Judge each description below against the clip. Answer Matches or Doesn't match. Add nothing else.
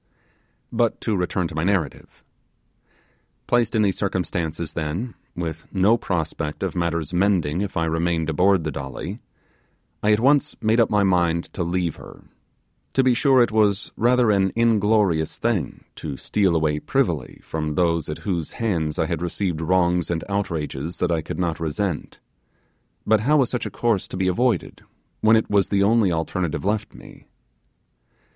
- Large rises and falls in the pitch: Doesn't match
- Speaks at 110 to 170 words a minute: Matches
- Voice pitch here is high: Doesn't match